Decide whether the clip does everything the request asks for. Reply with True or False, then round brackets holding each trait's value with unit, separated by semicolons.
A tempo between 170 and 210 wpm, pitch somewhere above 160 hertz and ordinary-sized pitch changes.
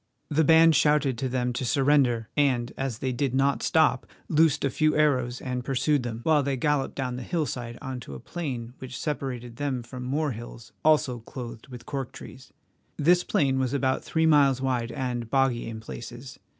False (190 wpm; 130 Hz; 3.1 semitones)